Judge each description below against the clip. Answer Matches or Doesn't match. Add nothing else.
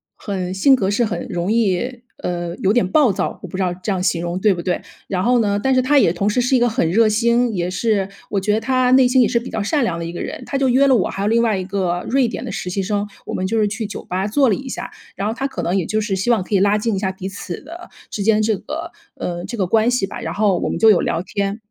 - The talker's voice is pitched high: Matches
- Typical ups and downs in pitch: Matches